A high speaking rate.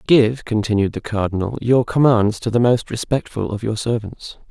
No: average, 175 wpm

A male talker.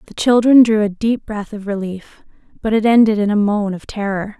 No: female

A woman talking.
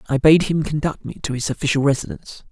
No: male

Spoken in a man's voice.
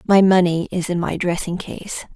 No: female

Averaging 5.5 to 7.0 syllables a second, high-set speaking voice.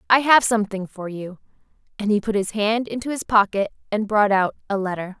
Yes: 5.7 syllables/s; high, 210 Hz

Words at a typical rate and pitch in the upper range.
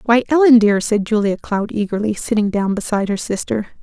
Yes: average, 190 wpm; high, 215 Hz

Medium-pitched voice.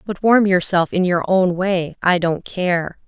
Yes: medium, 180 Hz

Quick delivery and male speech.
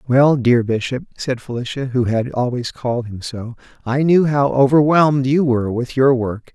No: average, 185 wpm; male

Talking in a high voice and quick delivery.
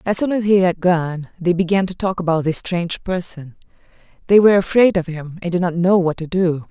No: medium, 175 Hz; fast, 235 wpm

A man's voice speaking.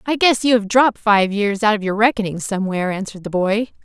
No: female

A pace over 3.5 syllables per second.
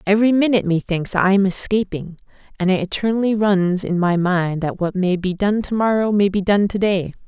Yes: 5.4 syllables/s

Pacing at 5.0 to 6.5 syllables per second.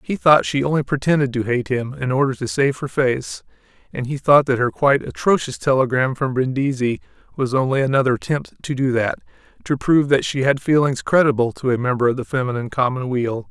Yes: 5.9 syllables/s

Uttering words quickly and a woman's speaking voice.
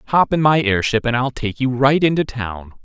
No: fast, 230 wpm; male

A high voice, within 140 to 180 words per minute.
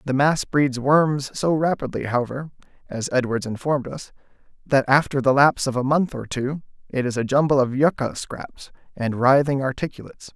No: low, 135 Hz; average, 175 wpm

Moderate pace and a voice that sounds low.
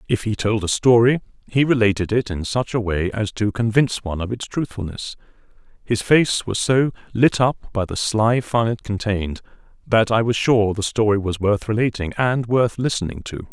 Yes: average, 195 wpm; low, 110 Hz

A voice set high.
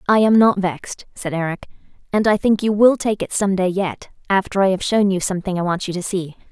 Yes: high, 195 Hz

